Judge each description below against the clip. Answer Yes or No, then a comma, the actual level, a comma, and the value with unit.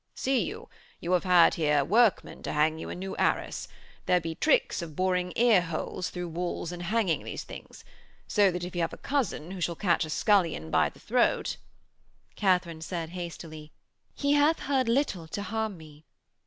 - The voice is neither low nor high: Yes, medium, 180 Hz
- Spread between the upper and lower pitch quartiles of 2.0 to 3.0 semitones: No, average, 3.9 semitones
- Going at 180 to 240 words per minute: Yes, average, 185 wpm